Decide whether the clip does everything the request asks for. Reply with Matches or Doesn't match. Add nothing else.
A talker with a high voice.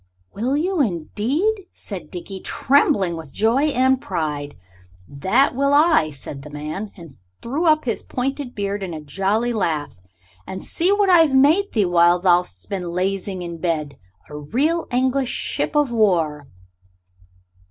Matches